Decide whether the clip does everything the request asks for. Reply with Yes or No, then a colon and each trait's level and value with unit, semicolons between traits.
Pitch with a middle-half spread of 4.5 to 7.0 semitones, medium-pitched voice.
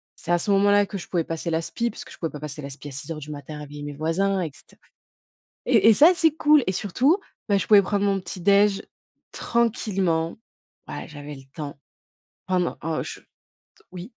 Yes: average, 4.8 semitones; medium, 180 Hz